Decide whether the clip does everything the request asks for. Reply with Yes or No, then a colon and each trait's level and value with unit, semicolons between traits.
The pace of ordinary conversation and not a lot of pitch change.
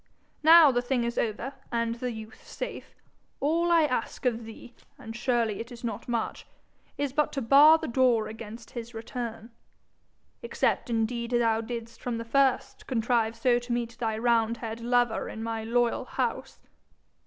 Yes: average, 165 wpm; narrow, 1.7 semitones